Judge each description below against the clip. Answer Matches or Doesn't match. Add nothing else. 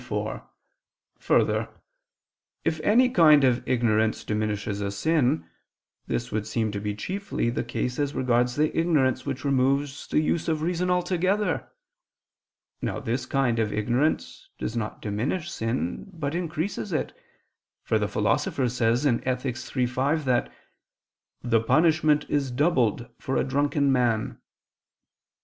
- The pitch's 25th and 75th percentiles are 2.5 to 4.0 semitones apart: Doesn't match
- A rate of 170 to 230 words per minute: Doesn't match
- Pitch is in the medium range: Doesn't match